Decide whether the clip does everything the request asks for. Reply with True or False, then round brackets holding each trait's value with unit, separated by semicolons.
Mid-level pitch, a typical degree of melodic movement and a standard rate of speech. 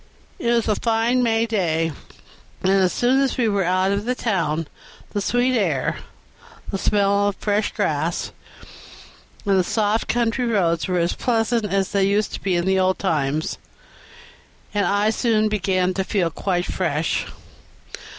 False (200 Hz; 3.4 semitones; 165 wpm)